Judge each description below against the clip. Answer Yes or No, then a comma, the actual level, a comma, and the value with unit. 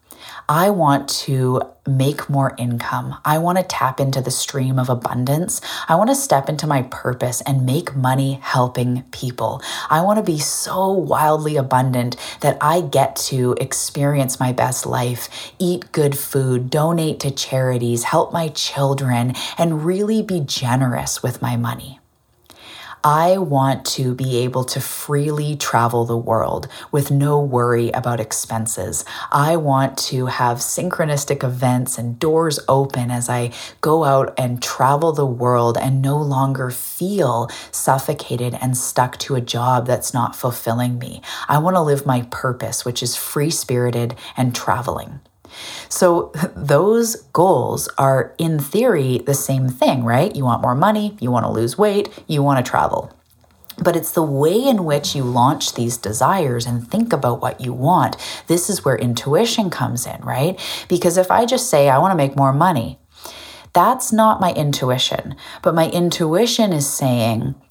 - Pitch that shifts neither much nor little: Yes, average, 3.9 semitones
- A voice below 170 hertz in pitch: Yes, low, 135 Hz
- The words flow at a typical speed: Yes, average, 160 wpm